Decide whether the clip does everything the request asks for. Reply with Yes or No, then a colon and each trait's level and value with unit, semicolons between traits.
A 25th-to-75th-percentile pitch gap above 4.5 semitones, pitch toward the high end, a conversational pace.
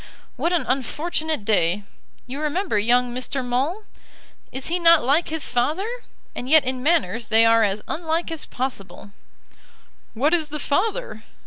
Yes: average, 5.3 semitones; very high, 275 Hz; average, 150 wpm